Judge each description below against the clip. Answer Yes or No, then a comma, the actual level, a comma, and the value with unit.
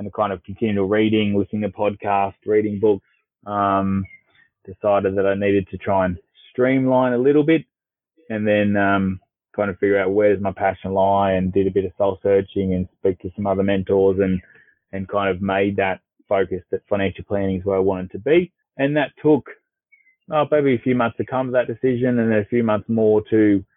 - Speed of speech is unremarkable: No, fast, 210 wpm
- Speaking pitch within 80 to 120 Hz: Yes, low, 100 Hz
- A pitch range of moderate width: Yes, average, 3.3 semitones